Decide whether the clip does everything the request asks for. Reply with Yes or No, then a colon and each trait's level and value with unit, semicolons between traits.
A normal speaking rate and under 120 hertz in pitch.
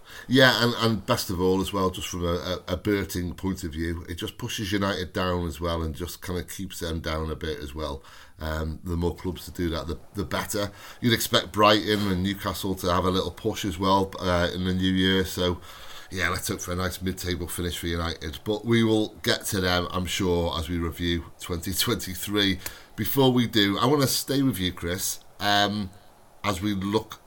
No: fast, 220 wpm; very low, 95 Hz